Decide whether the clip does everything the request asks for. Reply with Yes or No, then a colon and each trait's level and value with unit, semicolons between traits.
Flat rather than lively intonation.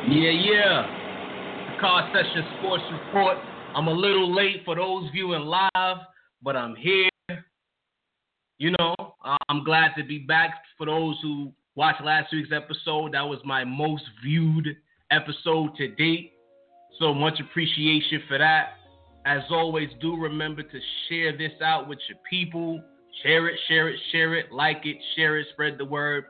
Yes: narrow, 2.3 semitones